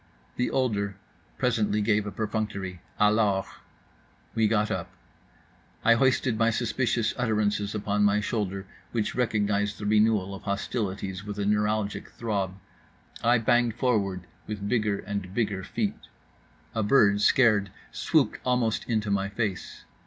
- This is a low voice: Yes, low, 105 Hz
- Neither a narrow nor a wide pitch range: No, narrow, 2.0 semitones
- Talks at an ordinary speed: No, slow, 130 wpm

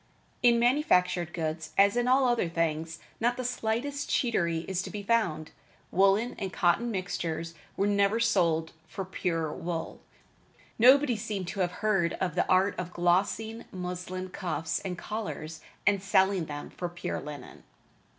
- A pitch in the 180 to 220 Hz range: Yes, medium, 185 Hz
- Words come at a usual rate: Yes, average, 150 wpm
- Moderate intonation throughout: Yes, average, 4.5 semitones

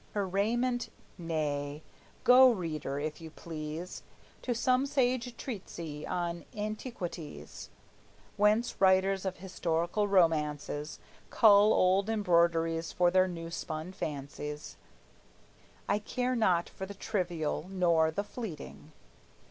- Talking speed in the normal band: No, slow, 110 wpm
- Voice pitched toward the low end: No, medium, 180 Hz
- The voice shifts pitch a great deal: No, average, 4.5 semitones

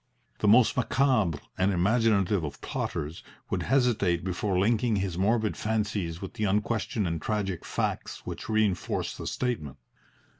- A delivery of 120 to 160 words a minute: Yes, average, 140 wpm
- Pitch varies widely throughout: No, average, 3.6 semitones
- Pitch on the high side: No, low, 105 Hz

